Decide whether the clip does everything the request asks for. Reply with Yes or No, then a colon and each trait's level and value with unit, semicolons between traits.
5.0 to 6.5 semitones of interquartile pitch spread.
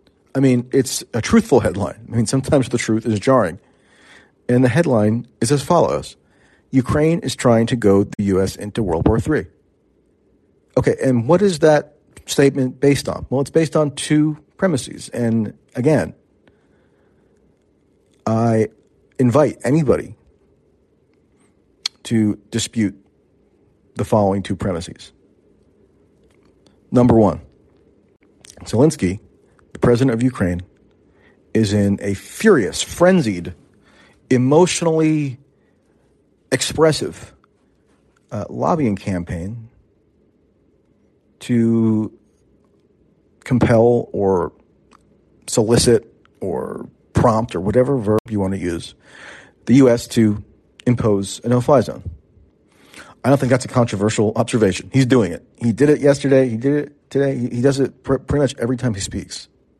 No: average, 4.5 semitones